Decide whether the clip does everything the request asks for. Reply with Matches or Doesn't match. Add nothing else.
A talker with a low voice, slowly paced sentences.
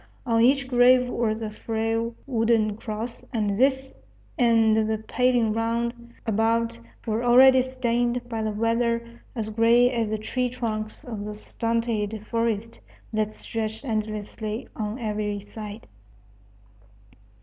Doesn't match